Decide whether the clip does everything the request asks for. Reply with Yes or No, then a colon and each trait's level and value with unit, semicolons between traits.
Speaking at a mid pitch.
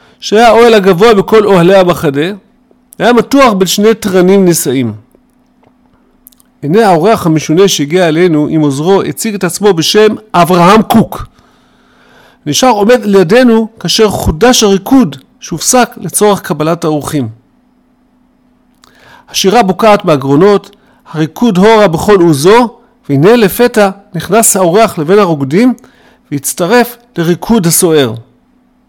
No: high, 200 Hz